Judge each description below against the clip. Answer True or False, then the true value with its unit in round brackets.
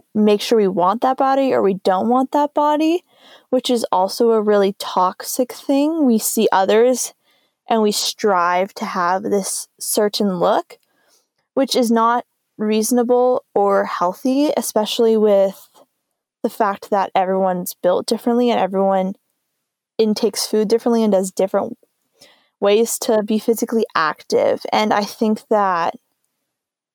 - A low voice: False (220 Hz)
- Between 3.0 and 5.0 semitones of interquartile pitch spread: True (4.2 semitones)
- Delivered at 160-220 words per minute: False (135 wpm)